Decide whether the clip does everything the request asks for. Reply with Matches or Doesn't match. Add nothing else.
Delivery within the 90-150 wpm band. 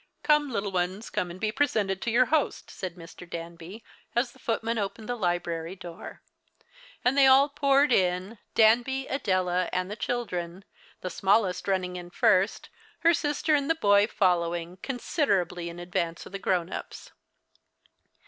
Doesn't match